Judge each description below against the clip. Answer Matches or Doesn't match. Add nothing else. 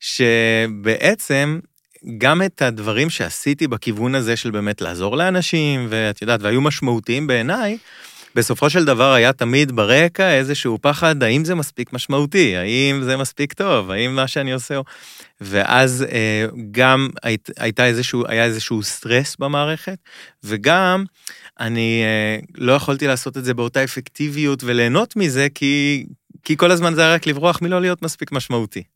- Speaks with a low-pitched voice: Matches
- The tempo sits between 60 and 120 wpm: Doesn't match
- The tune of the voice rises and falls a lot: Doesn't match